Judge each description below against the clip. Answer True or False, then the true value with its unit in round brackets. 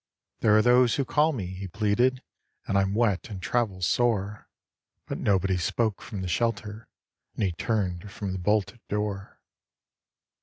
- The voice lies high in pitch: False (105 Hz)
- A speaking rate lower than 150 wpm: False (165 wpm)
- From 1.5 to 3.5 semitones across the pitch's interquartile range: True (3.2 semitones)